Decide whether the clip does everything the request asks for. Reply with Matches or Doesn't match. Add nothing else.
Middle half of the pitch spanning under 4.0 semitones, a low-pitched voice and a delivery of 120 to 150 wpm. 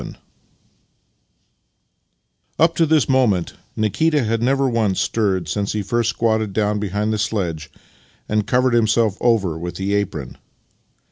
Matches